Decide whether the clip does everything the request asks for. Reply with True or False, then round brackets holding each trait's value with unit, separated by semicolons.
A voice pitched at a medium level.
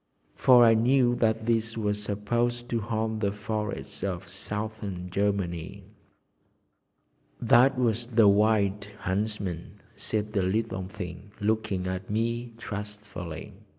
False (105 Hz)